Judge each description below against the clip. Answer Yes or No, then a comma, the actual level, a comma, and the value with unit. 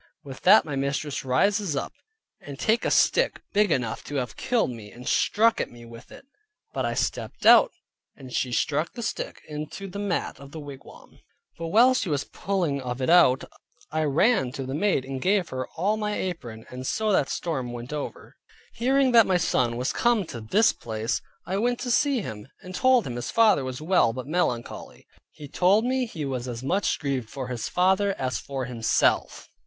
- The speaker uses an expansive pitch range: Yes, wide, 8.0 semitones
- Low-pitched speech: No, medium, 150 Hz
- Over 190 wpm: Yes, average, 200 wpm